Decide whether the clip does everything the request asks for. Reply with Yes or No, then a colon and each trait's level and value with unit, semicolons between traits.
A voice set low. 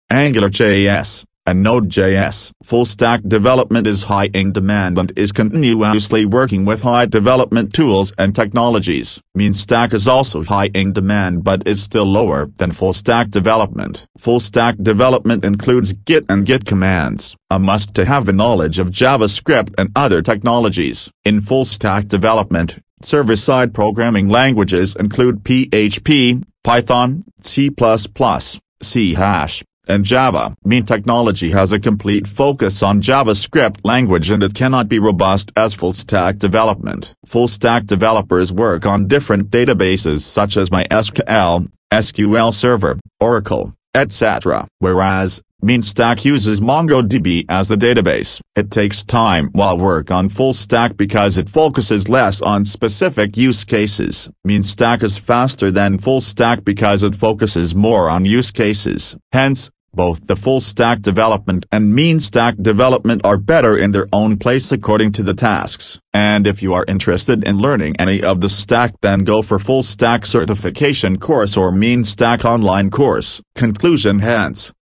Yes: low, 105 Hz